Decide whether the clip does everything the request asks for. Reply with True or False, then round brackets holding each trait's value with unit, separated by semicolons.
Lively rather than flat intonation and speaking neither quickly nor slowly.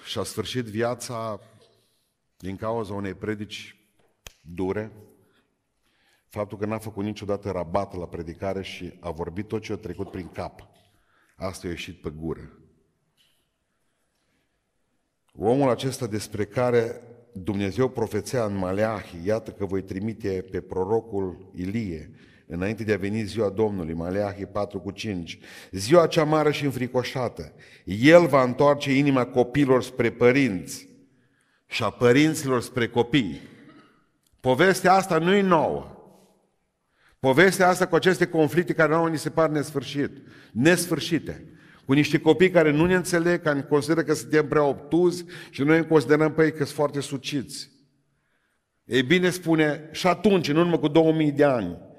True (7.3 semitones; 145 wpm)